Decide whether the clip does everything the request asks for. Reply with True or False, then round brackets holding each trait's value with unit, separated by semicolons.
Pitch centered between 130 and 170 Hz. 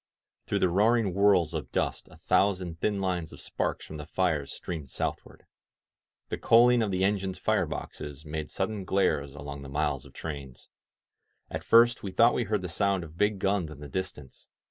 False (90 Hz)